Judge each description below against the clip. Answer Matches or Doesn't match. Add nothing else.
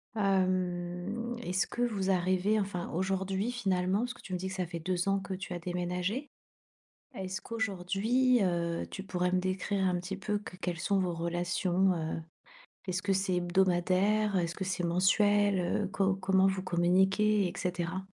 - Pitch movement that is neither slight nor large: Doesn't match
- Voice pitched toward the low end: Doesn't match